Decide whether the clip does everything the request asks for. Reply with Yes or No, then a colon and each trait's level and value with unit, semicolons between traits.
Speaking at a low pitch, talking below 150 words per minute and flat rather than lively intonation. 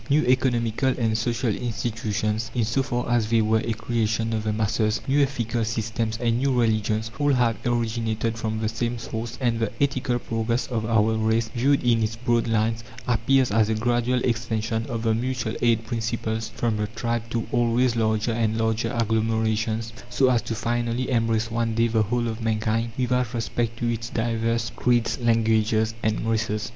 No: low, 115 Hz; average, 180 wpm; narrow, 1.4 semitones